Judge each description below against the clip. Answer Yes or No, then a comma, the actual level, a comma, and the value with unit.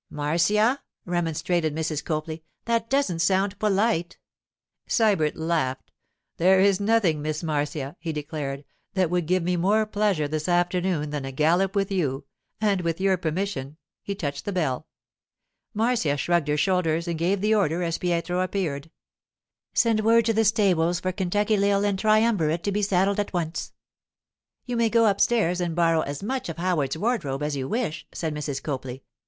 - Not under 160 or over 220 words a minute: Yes, average, 165 wpm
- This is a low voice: No, medium, 175 Hz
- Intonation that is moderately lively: Yes, average, 4.5 semitones